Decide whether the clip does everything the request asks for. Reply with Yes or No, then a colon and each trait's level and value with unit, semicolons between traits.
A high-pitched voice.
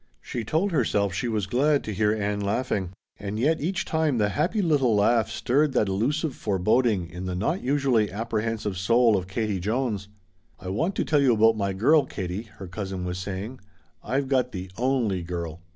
No: low, 110 Hz